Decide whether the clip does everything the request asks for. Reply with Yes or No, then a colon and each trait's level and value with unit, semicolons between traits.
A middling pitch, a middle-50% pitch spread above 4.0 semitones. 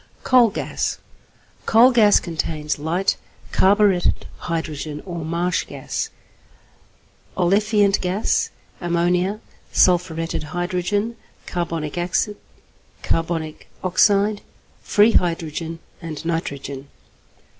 No: medium, 175 Hz; average, 3.6 semitones